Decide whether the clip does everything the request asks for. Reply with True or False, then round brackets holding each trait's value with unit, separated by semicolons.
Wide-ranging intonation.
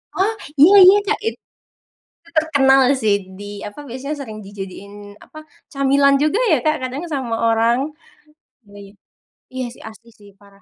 True (6.2 semitones)